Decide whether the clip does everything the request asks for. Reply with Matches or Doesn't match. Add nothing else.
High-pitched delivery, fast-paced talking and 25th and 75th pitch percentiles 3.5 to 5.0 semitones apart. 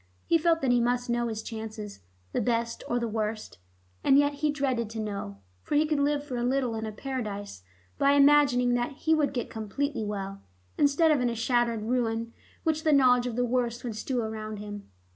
Matches